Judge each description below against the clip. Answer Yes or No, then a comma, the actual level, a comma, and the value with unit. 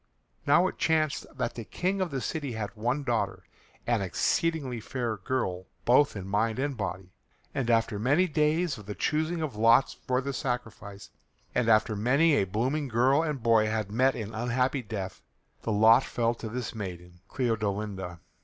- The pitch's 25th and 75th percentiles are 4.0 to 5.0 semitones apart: Yes, average, 4.5 semitones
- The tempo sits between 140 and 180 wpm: Yes, average, 175 wpm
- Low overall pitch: Yes, low, 115 Hz